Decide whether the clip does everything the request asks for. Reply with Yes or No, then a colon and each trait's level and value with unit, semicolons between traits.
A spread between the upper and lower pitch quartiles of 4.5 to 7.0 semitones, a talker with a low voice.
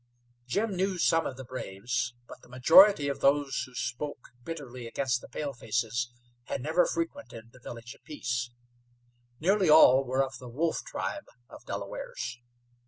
Yes: average, 5.1 semitones; low, 130 Hz